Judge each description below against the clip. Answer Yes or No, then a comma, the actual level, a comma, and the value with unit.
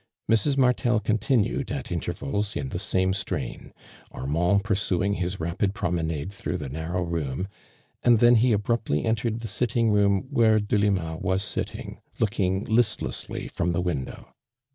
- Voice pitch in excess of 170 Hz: No, low, 100 Hz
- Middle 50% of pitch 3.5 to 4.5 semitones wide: Yes, average, 4.1 semitones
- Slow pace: No, average, 145 wpm